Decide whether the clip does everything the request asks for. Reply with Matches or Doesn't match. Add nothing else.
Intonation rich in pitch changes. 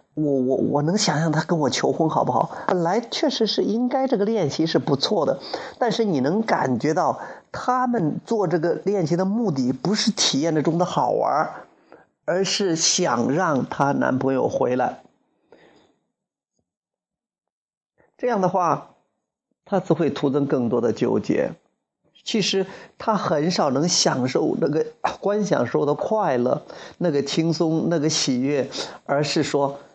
Matches